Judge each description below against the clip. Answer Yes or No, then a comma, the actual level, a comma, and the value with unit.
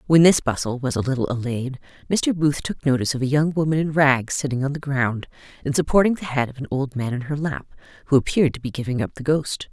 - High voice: No, medium, 140 Hz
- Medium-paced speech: No, fast, 245 wpm